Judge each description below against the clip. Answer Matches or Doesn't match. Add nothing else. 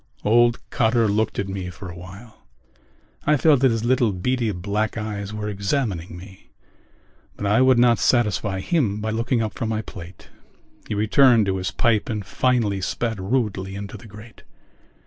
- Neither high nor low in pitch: Doesn't match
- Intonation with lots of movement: Doesn't match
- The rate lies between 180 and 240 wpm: Doesn't match